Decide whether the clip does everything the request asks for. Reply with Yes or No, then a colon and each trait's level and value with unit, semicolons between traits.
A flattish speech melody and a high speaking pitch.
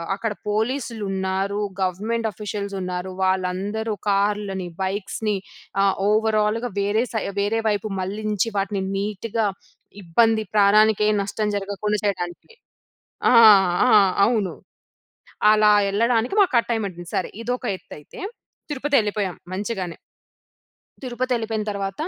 Yes: narrow, 2.3 semitones; high, 210 Hz